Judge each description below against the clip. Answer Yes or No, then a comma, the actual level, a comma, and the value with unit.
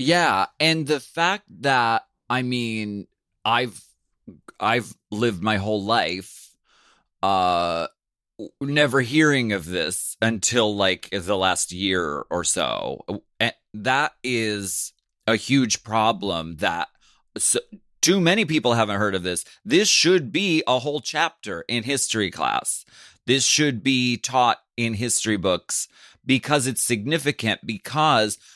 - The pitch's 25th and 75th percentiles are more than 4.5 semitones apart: Yes, average, 5.0 semitones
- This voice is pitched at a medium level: No, low, 120 Hz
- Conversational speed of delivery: No, slow, 125 wpm